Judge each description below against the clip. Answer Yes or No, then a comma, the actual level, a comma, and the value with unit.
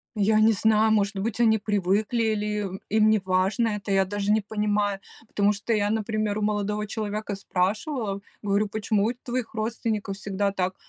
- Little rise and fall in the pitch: Yes, narrow, 1.5 semitones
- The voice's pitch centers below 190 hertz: No, high, 210 Hz